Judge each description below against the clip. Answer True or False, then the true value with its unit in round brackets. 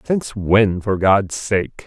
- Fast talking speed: False (160 wpm)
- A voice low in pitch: True (105 Hz)